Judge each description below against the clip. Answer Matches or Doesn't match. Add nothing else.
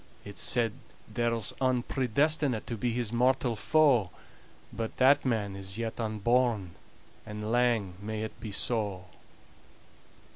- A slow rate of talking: Matches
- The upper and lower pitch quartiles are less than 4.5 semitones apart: Matches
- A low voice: Matches